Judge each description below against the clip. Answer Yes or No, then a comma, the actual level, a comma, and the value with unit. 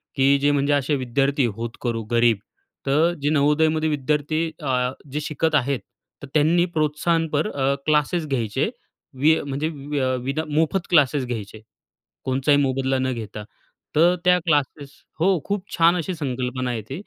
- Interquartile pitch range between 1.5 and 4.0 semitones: Yes, average, 3.1 semitones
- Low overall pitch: No, medium, 145 Hz